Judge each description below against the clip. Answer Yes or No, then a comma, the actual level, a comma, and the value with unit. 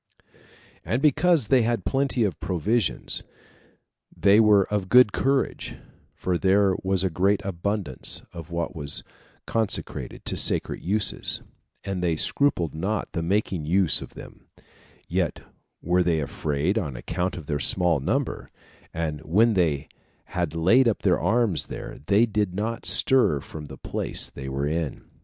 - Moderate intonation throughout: Yes, average, 4.7 semitones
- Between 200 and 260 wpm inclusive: No, average, 150 wpm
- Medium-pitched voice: No, very low, 95 Hz